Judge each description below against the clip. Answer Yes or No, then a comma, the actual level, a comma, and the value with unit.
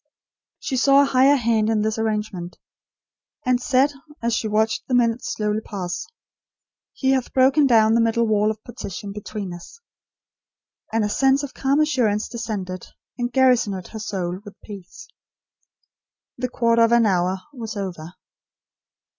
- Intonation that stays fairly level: No, average, 3.5 semitones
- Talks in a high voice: Yes, high, 225 Hz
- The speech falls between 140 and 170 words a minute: Yes, average, 150 wpm